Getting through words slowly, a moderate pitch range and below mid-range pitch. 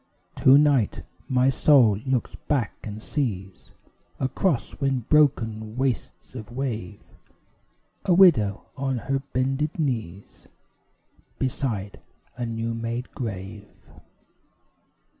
Yes: slow, 100 wpm; average, 4.0 semitones; low, 125 Hz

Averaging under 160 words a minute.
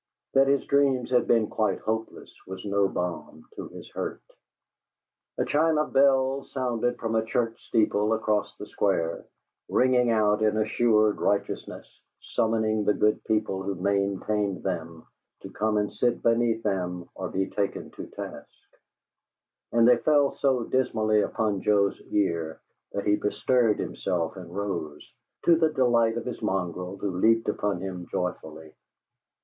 Yes: average, 150 wpm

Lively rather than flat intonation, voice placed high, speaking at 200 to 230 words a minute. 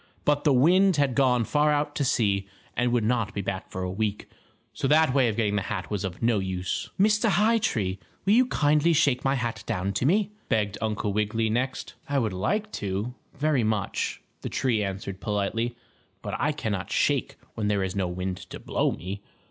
No: wide, 6.5 semitones; low, 115 Hz; fast, 205 wpm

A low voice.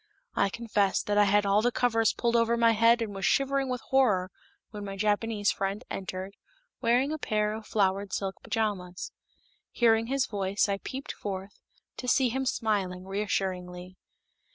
No: high, 210 Hz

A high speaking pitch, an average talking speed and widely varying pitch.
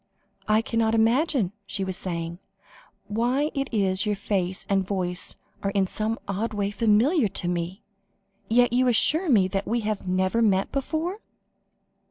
No: high, 210 Hz; average, 160 wpm; average, 4.0 semitones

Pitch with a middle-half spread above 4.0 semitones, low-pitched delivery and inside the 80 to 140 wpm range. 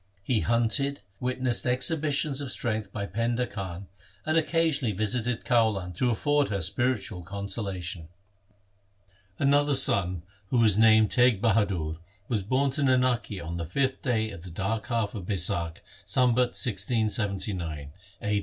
Yes: average, 4.6 semitones; low, 110 Hz; slow, 135 wpm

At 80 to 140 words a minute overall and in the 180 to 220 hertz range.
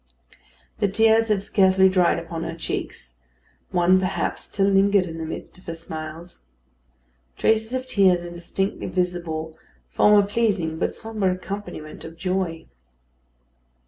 Yes: slow, 135 wpm; medium, 185 Hz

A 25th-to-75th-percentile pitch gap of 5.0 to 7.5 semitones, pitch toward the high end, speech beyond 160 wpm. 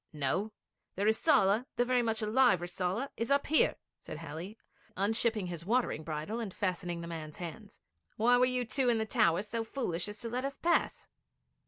Yes: average, 5.3 semitones; high, 215 Hz; average, 185 wpm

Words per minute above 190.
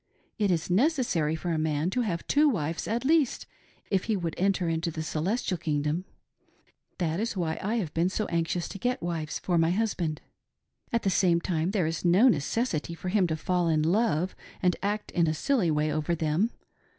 Yes: average, 200 wpm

